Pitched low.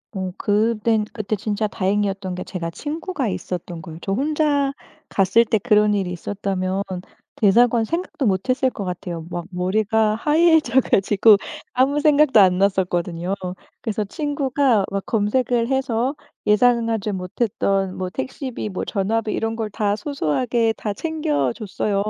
No: high, 215 Hz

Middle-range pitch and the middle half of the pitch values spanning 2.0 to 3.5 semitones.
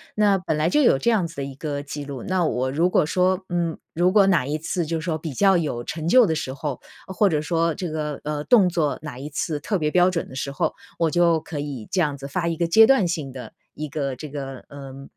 No: medium, 155 Hz; average, 3.9 semitones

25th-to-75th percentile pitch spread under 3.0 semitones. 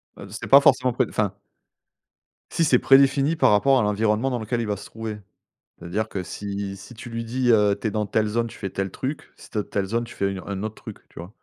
No: average, 3.4 semitones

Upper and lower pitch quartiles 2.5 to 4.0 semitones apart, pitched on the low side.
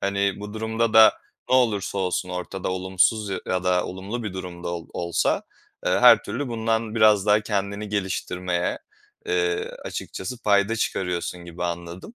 Yes: average, 3.5 semitones; low, 100 Hz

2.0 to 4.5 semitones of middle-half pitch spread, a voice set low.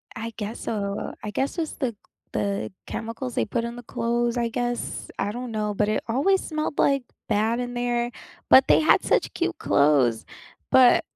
No: average, 2.8 semitones; high, 235 Hz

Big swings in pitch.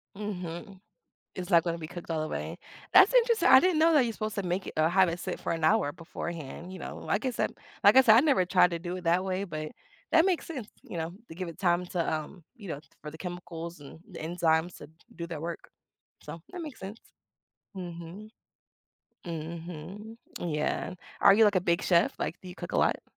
No: average, 3.7 semitones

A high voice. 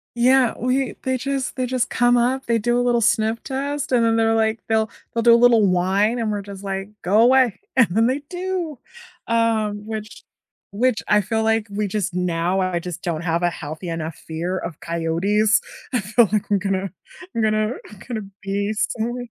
Yes: high, 220 Hz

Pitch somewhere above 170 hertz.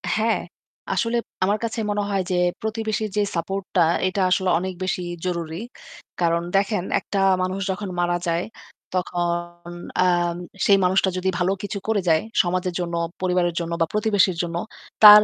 Yes: medium, 185 Hz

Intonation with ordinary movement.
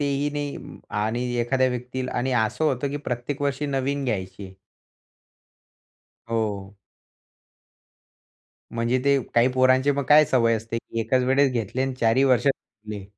Yes: average, 3.1 semitones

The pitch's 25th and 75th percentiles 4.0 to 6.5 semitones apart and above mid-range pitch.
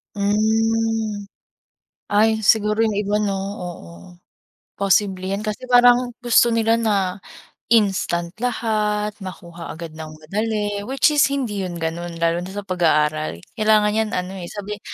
No: average, 3.5 semitones; high, 205 Hz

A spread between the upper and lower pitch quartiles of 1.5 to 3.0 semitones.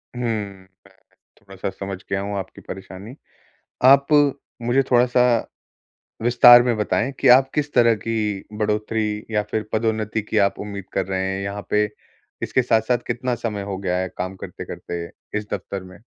No: average, 3.4 semitones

